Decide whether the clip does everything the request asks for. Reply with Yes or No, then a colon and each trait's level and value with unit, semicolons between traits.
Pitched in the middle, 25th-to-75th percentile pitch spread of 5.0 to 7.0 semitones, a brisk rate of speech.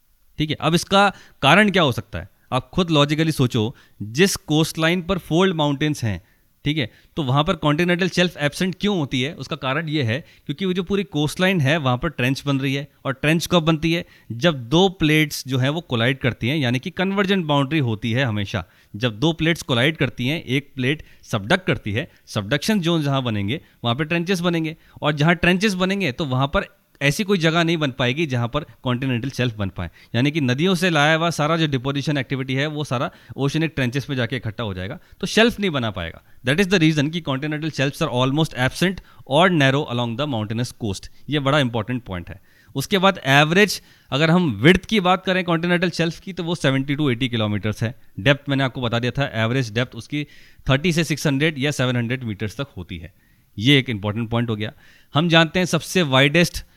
Yes: medium, 145 Hz; average, 5.3 semitones; fast, 210 wpm